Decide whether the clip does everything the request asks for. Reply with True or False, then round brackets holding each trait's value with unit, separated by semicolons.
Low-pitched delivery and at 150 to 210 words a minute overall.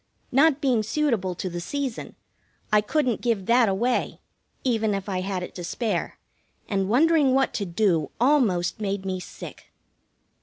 False (215 Hz; 155 wpm)